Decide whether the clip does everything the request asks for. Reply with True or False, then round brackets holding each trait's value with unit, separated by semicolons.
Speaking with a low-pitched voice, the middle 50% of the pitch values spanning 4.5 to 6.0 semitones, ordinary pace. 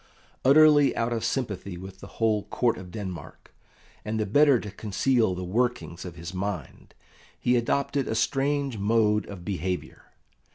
True (110 Hz; 4.9 semitones; 155 wpm)